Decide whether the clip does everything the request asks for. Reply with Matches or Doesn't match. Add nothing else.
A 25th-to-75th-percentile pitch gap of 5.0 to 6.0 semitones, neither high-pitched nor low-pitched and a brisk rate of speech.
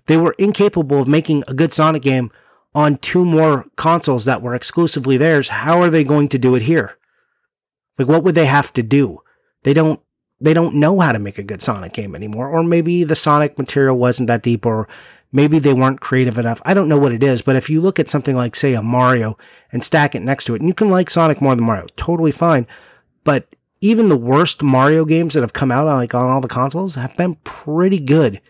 Doesn't match